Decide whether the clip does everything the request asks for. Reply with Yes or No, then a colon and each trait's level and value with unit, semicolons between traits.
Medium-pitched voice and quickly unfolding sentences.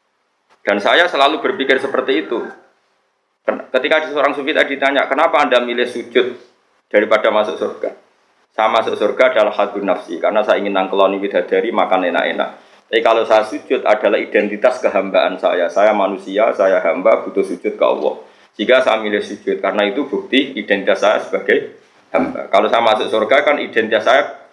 Yes: medium, 155 Hz; fast, 160 wpm